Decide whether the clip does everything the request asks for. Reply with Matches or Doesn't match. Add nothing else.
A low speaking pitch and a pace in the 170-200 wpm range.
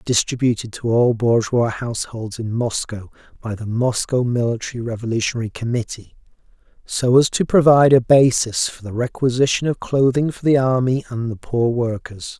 Doesn't match